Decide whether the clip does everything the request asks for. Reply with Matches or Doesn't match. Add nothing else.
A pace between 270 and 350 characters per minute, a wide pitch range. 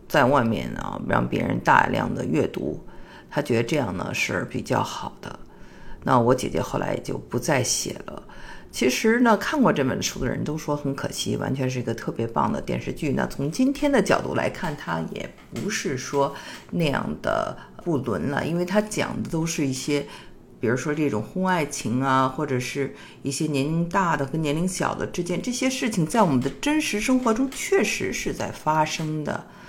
Matches